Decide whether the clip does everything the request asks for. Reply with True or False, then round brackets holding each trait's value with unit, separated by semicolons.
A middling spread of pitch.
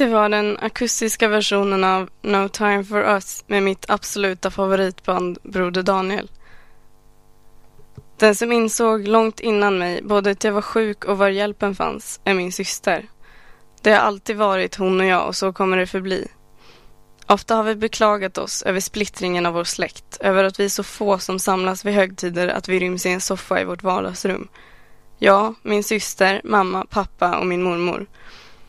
False (2.0 semitones)